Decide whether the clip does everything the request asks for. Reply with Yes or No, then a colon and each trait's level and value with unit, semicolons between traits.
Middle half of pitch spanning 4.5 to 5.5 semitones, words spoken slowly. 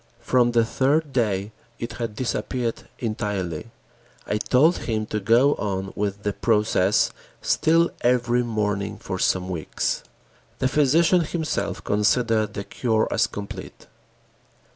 No: average, 3.6 semitones; slow, 125 wpm